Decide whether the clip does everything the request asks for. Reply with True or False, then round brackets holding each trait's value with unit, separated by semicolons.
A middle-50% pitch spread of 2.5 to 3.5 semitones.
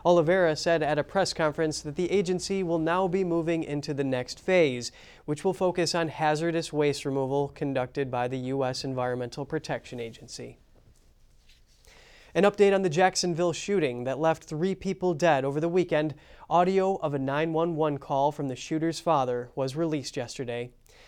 False (4.2 semitones)